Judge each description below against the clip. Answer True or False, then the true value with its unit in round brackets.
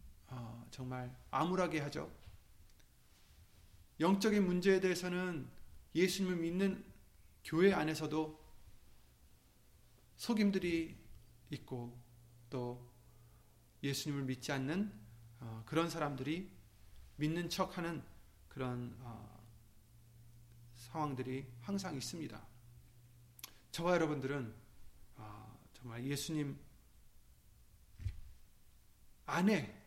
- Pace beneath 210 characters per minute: True (175 characters per minute)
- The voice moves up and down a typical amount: False (6.8 semitones)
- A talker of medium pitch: False (120 Hz)